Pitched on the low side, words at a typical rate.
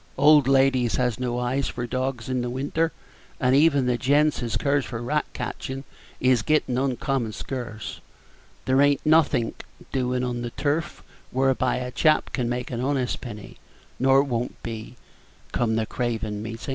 Yes: low, 130 Hz; average, 160 wpm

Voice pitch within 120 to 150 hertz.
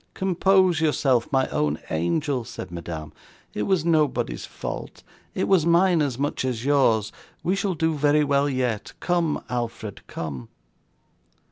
Yes: medium, 140 Hz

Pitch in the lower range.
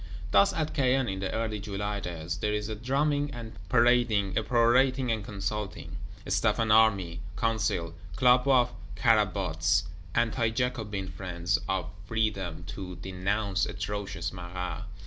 Yes: low, 105 Hz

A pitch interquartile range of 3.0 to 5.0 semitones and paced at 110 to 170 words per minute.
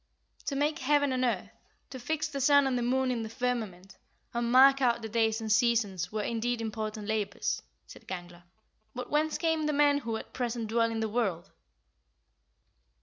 No: average, 3.6 semitones; average, 190 wpm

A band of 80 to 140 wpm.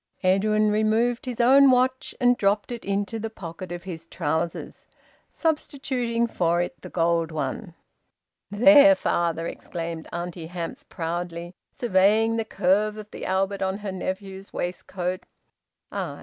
Yes: slow, 135 wpm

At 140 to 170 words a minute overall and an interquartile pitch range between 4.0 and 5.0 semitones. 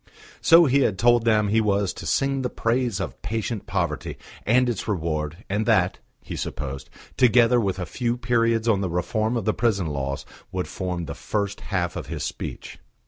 No: average, 190 wpm; average, 4.7 semitones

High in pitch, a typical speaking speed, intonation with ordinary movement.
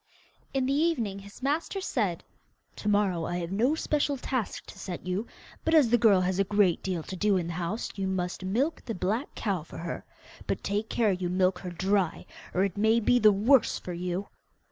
No: high, 200 Hz; fast, 210 wpm; average, 4.4 semitones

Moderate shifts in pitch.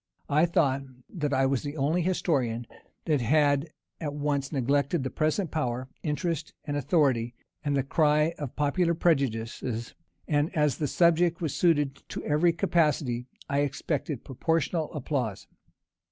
Yes: average, 3.0 semitones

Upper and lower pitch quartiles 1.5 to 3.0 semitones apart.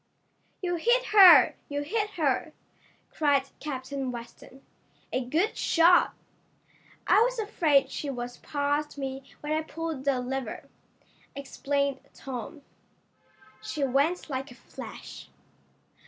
No: average, 3.6 semitones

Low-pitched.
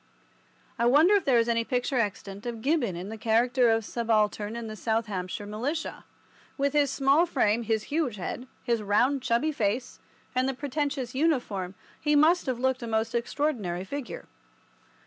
No: high, 240 Hz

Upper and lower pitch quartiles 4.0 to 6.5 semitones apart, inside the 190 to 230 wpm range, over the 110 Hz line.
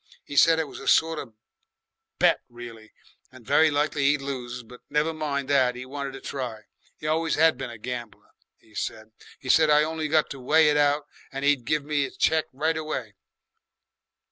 No: average, 3.6 semitones; average, 195 wpm; medium, 140 Hz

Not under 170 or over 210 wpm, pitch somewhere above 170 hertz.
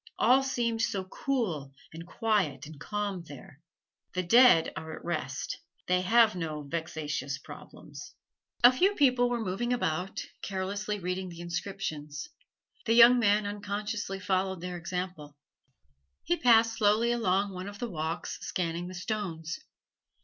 No: average, 140 wpm; high, 190 Hz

